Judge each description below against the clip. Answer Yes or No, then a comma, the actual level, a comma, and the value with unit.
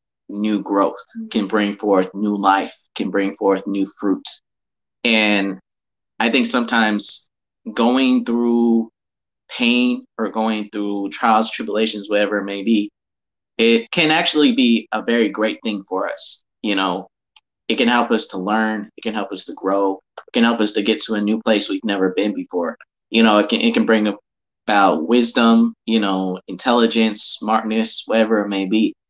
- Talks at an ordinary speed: Yes, average, 170 wpm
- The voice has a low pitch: Yes, low, 105 Hz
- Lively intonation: No, narrow, 2.6 semitones